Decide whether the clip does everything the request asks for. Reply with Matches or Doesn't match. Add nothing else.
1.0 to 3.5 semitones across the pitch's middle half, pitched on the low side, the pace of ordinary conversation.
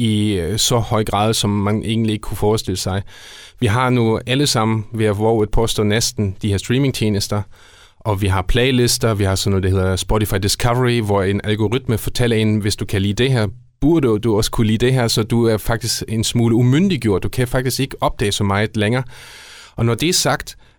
Matches